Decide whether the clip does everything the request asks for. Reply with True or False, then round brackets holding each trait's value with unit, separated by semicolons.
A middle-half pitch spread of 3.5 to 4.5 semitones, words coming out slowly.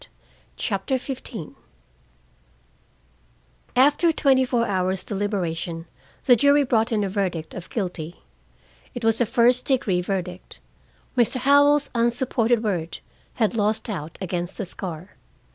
False (5.3 semitones; 120 wpm)